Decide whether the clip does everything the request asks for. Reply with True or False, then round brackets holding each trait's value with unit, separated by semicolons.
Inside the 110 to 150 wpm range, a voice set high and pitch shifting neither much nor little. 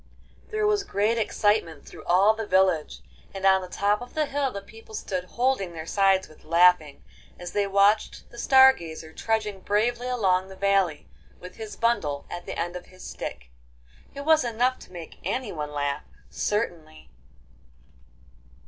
False (165 wpm; 195 Hz; 4.7 semitones)